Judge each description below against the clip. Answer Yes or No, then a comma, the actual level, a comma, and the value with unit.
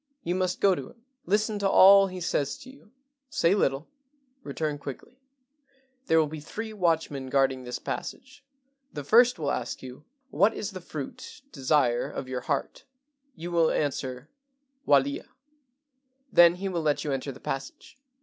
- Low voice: No, medium, 160 Hz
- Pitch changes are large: Yes, wide, 6.2 semitones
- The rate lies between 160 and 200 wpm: Yes, average, 170 wpm